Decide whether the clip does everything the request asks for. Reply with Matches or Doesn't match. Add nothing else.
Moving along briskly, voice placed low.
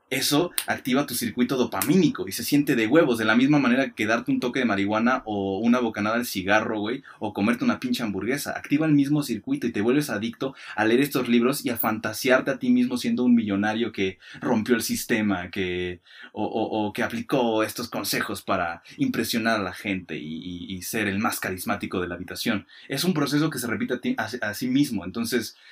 Matches